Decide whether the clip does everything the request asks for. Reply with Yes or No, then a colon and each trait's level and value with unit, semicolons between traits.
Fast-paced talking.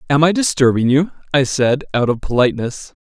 No: average, 180 wpm